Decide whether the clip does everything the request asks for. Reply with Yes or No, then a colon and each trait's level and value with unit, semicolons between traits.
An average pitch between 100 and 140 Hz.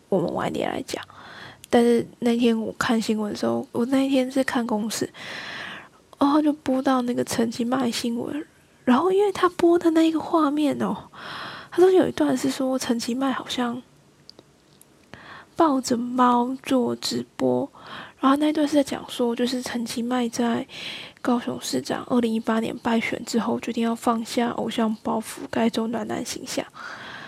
No: high, 245 Hz